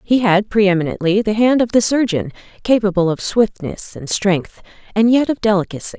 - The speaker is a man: No, female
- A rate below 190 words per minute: Yes, average, 180 wpm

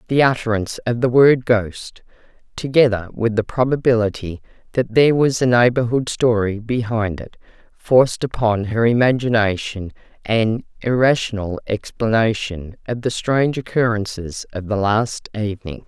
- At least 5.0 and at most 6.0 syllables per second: No, 4.8 syllables/s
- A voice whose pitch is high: No, low, 115 Hz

